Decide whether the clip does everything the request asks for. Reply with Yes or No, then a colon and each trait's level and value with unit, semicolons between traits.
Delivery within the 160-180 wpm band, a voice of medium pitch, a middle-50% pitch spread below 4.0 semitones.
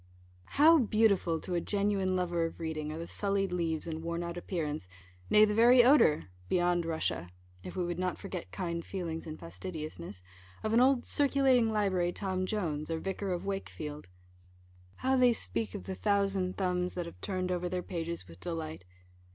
Yes: average, 175 wpm; medium, 180 Hz; average, 3.6 semitones